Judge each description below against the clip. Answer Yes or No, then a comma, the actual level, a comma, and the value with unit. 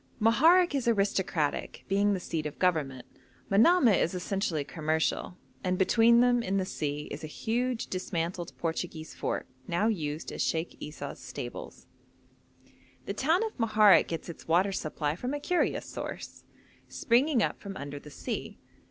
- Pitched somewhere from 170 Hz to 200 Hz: Yes, medium, 185 Hz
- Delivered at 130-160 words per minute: Yes, average, 150 wpm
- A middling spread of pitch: No, wide, 6.4 semitones